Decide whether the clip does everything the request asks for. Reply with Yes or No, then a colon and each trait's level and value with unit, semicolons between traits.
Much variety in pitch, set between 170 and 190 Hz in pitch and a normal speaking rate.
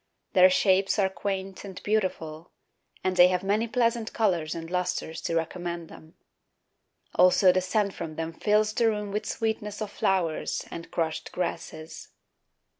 No: average, 3.6 semitones; medium, 185 Hz; average, 150 wpm